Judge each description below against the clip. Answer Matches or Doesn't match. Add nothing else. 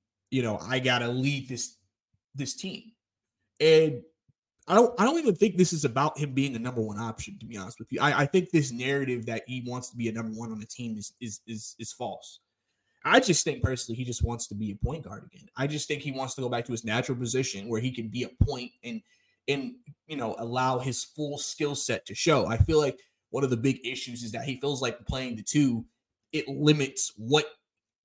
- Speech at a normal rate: Doesn't match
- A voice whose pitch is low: Matches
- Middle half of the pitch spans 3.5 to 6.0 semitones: Matches